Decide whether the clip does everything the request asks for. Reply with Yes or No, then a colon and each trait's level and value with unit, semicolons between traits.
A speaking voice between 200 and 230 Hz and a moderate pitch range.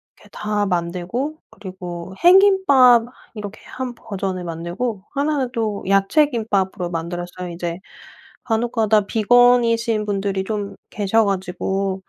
Yes: high, 205 Hz; average, 4.2 semitones